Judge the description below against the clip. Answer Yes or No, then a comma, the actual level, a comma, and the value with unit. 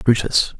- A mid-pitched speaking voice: No, low, 115 Hz